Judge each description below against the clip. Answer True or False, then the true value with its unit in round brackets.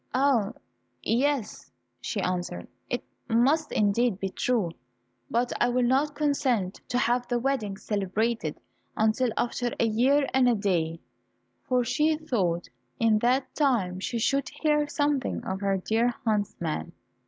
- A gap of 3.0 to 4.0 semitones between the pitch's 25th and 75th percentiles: False (4.6 semitones)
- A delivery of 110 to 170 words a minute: True (140 wpm)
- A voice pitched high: True (240 Hz)